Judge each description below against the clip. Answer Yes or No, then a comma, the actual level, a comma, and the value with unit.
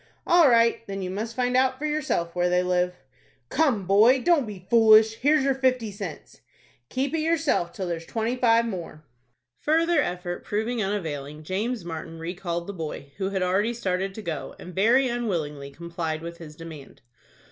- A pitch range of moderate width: No, wide, 6.3 semitones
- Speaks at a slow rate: No, average, 175 wpm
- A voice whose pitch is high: Yes, high, 195 Hz